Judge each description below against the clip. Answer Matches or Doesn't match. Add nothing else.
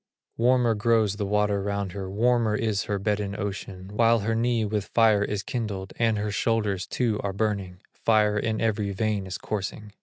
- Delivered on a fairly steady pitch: Matches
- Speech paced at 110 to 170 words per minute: Doesn't match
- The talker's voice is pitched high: Doesn't match